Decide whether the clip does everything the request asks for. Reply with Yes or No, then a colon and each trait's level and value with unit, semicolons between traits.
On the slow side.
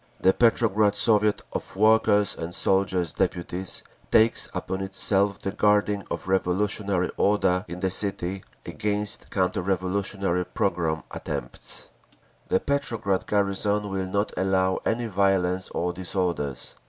Yes: slow, 125 wpm